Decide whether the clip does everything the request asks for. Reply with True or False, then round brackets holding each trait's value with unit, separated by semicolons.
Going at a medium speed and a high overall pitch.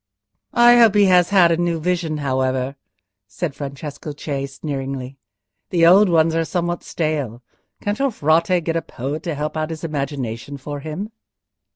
False (165 wpm; 155 Hz)